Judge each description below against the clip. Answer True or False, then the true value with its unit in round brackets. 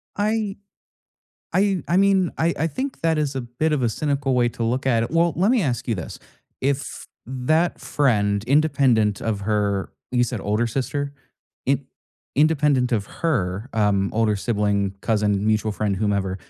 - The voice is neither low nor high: False (125 Hz)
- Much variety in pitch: True (6.5 semitones)